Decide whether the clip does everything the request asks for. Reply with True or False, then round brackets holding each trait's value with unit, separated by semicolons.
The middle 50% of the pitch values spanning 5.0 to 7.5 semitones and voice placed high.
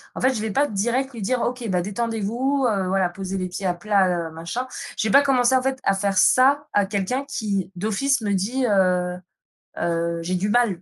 True (5.3 semitones; 205 Hz)